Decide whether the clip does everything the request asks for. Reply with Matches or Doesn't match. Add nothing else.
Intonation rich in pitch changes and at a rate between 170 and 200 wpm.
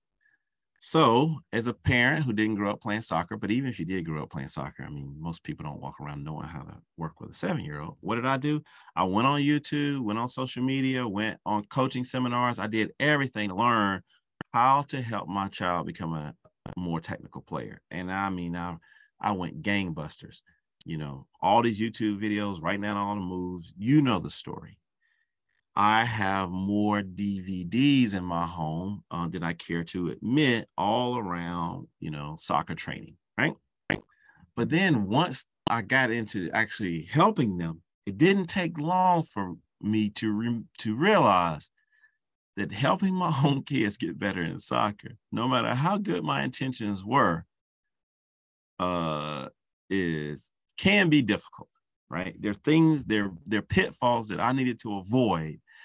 Matches